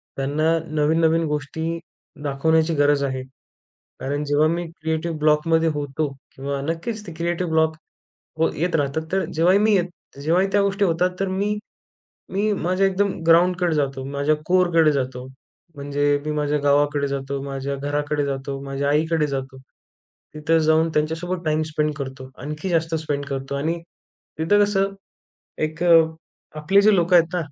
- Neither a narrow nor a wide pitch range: Yes, average, 3.0 semitones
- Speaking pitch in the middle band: Yes, medium, 155 Hz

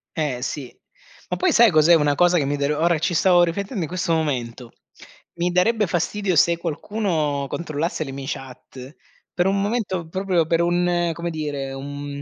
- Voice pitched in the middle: Yes, medium, 165 Hz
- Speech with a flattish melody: No, average, 3.8 semitones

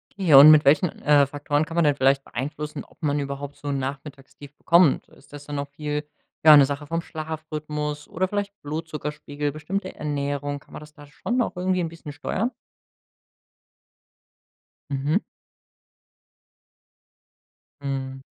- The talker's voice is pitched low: No, medium, 150 Hz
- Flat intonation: Yes, narrow, 1.8 semitones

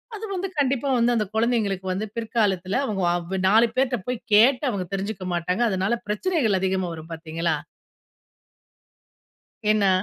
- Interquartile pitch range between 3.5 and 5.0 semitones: Yes, average, 4.2 semitones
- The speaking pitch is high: Yes, high, 210 Hz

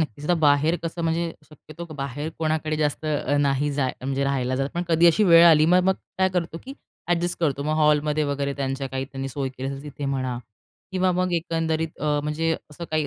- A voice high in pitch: No, medium, 150 Hz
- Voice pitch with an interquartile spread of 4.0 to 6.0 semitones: No, average, 3.0 semitones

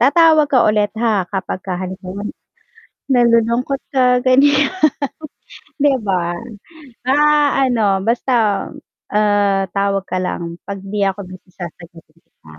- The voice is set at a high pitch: Yes, high, 210 Hz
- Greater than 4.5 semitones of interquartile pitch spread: Yes, average, 5.2 semitones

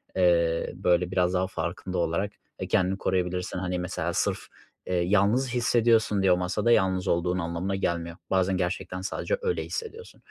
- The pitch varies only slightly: Yes, narrow, 1.9 semitones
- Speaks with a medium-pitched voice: No, very low, 90 Hz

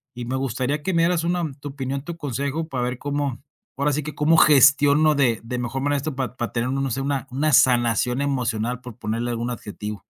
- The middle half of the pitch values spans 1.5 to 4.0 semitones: Yes, average, 2.9 semitones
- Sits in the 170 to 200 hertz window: No, low, 135 Hz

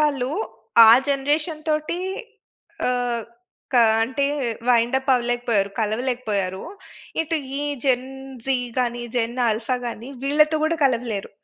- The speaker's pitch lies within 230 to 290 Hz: Yes, very high, 250 Hz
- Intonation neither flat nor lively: Yes, average, 3.2 semitones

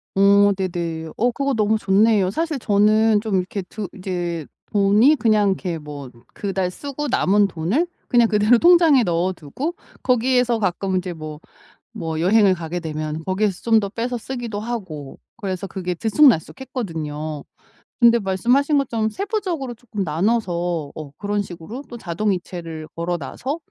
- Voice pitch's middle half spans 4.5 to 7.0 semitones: Yes, average, 5.3 semitones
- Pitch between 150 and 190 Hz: No, high, 200 Hz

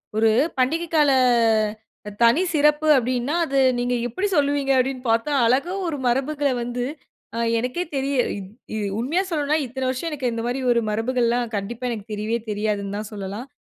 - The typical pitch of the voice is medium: No, very high, 250 Hz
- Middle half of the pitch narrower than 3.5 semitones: No, average, 3.8 semitones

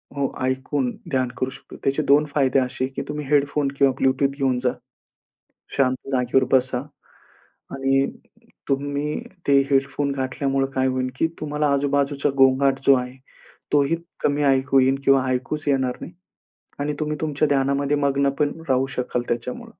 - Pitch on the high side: No, low, 135 Hz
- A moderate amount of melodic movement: No, narrow, 1.5 semitones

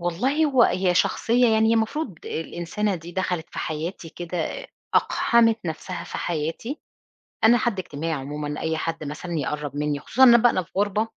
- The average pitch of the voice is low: No, medium, 180 Hz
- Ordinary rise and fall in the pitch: No, wide, 6.0 semitones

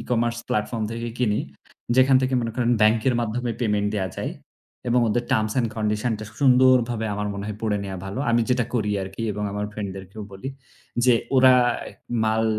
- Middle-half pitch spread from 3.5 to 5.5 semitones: No, average, 2.8 semitones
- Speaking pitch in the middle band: No, low, 115 Hz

